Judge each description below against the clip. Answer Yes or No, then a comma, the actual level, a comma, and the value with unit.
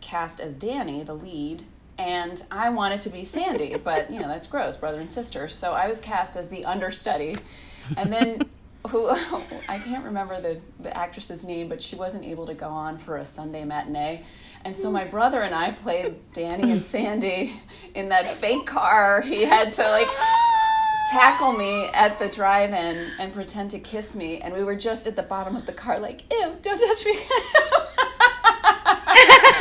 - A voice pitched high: Yes, high, 195 Hz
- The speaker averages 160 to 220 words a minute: Yes, average, 185 wpm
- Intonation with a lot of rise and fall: Yes, wide, 6.3 semitones